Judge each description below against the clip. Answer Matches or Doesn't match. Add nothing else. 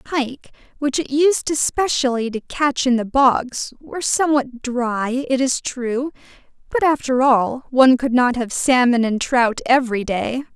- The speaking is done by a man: Doesn't match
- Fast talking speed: Doesn't match